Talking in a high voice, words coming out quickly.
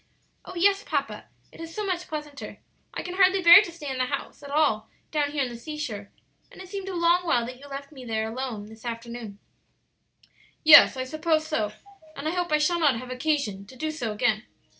Yes: very high, 285 Hz; fast, 220 wpm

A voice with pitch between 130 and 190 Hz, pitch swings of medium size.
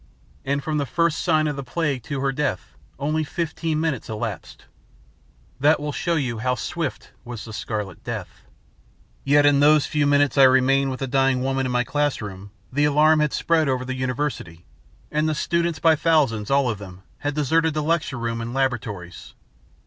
Yes: medium, 140 Hz; average, 3.4 semitones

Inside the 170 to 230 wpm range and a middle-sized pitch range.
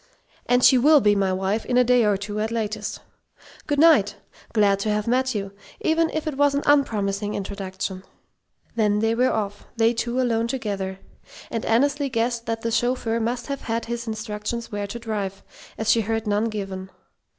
Yes: average, 185 wpm; average, 3.1 semitones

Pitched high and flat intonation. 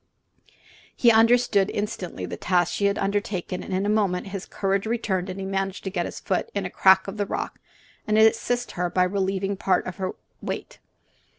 Yes: high, 195 Hz; narrow, 1.9 semitones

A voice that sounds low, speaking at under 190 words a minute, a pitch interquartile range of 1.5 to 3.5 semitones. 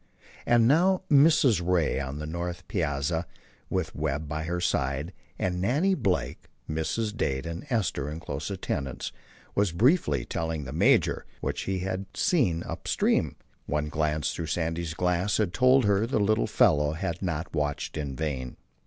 No: very low, 85 Hz; average, 160 wpm; average, 5.2 semitones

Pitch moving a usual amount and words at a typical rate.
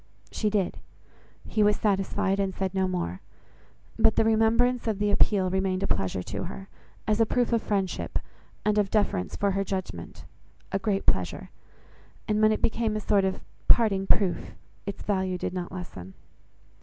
No: narrow, 2.3 semitones; average, 170 wpm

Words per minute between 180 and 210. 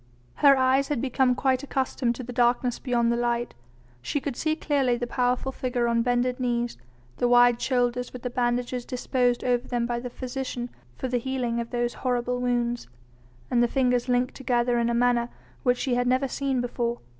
Yes: average, 190 wpm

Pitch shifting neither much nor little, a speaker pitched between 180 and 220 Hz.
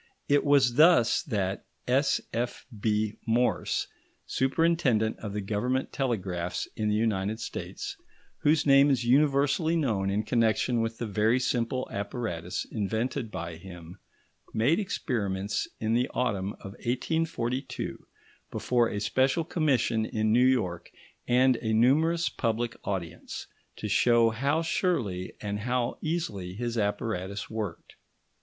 No: average, 4.2 semitones; low, 115 Hz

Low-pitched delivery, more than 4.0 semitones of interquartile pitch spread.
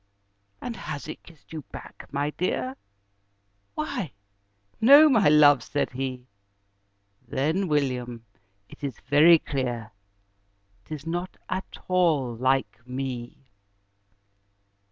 No: medium, 145 Hz; average, 4.4 semitones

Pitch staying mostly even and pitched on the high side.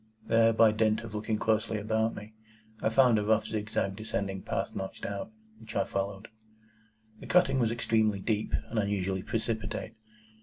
No: narrow, 1.6 semitones; low, 110 Hz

